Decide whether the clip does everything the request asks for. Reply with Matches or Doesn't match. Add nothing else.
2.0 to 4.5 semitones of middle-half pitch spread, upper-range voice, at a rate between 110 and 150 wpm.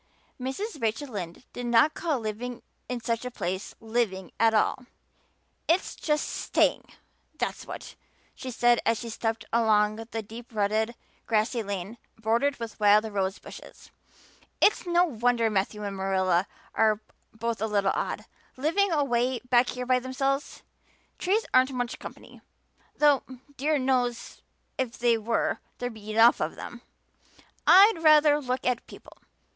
Matches